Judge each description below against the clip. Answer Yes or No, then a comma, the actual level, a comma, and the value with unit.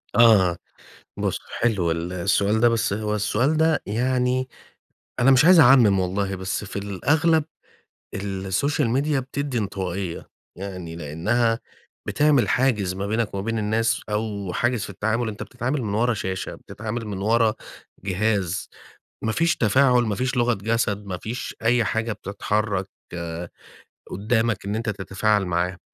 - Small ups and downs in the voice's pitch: No, average, 3.7 semitones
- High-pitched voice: No, low, 110 Hz